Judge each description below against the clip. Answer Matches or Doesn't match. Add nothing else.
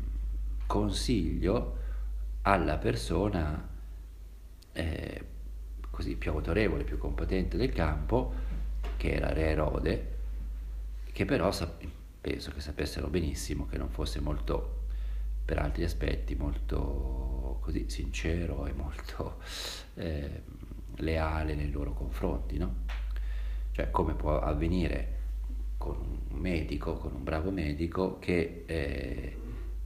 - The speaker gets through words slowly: Matches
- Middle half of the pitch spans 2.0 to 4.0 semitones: Doesn't match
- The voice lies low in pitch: Matches